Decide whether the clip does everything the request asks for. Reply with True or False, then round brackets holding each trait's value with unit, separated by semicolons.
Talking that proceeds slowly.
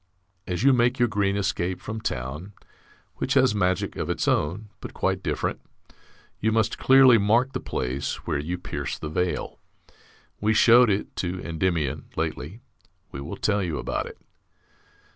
False (160 wpm)